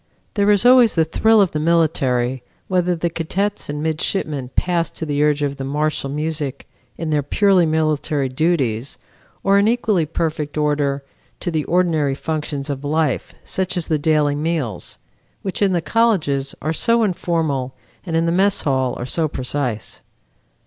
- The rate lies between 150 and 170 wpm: Yes, average, 165 wpm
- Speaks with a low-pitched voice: No, medium, 155 Hz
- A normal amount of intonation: Yes, average, 3.7 semitones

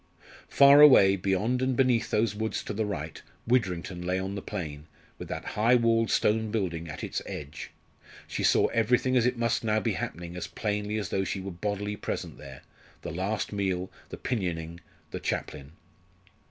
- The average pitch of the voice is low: Yes, low, 105 Hz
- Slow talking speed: No, average, 180 wpm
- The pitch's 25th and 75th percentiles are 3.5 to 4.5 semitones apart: Yes, average, 4.2 semitones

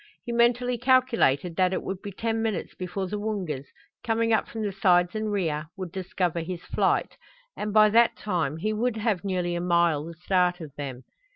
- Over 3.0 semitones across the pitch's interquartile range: Yes, average, 4.1 semitones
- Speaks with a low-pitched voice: No, high, 190 Hz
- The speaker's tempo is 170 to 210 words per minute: Yes, average, 195 wpm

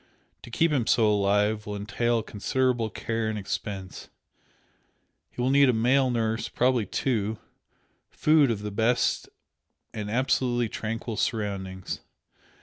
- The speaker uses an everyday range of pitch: Yes, average, 3.1 semitones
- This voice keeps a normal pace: No, slow, 130 wpm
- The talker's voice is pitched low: Yes, low, 115 Hz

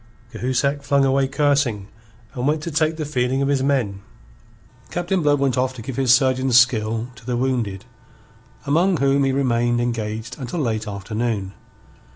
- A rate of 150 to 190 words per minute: Yes, average, 165 wpm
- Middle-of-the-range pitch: No, low, 130 Hz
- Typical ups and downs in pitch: Yes, average, 3.1 semitones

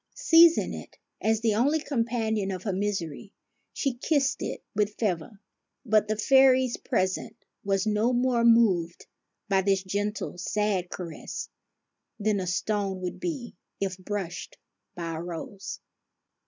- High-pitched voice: Yes, high, 210 Hz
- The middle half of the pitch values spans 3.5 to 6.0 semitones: Yes, average, 3.9 semitones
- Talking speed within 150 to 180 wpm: No, slow, 135 wpm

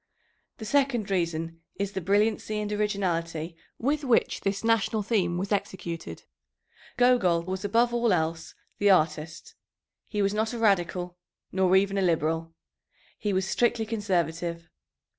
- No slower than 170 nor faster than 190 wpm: No, average, 140 wpm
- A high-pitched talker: Yes, high, 195 Hz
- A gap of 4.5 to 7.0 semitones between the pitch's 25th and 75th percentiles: No, average, 4.1 semitones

